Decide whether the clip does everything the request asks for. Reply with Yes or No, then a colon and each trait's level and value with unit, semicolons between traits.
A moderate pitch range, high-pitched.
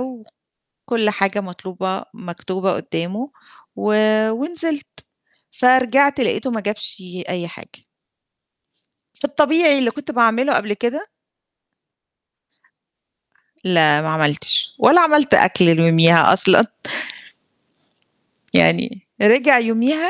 No: wide, 7.1 semitones; high, 225 Hz